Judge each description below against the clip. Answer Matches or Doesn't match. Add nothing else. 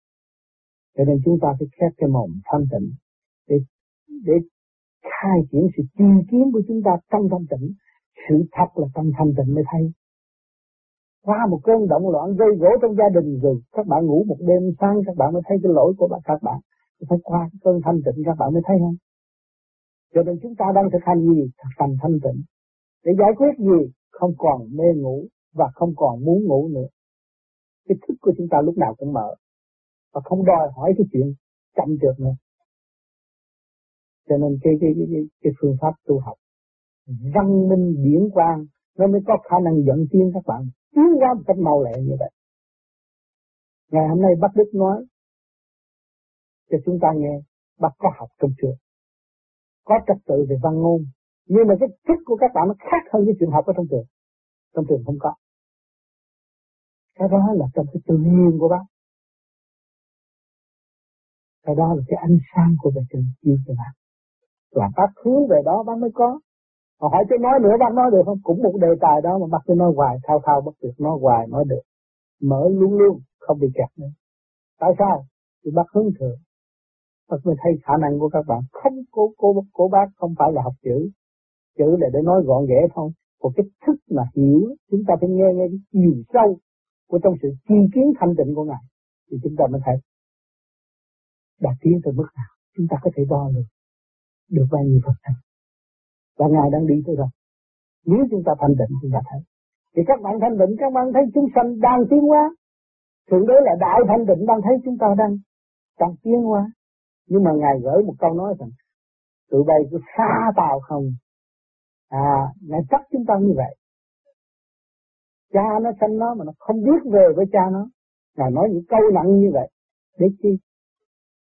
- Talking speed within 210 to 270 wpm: Doesn't match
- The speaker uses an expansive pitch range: Matches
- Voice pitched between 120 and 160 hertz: Doesn't match